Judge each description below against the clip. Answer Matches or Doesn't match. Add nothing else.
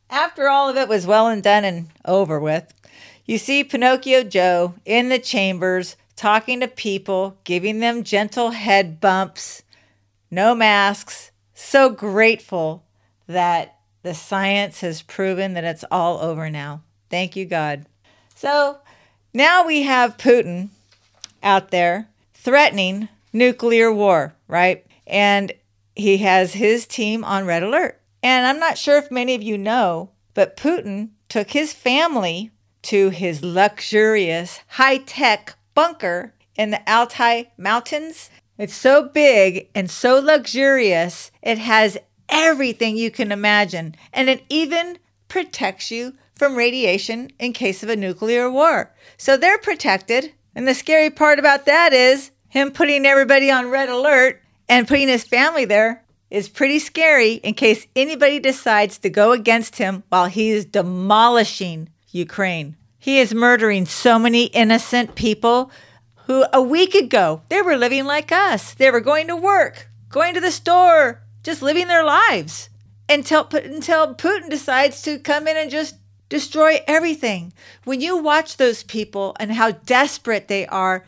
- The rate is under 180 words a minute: Matches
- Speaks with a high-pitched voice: Matches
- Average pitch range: Doesn't match